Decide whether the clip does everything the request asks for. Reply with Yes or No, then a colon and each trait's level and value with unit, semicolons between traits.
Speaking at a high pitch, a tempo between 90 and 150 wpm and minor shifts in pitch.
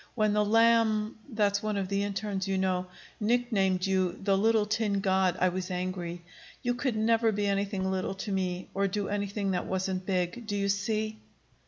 No: high, 200 Hz; average, 185 wpm; narrow, 2.3 semitones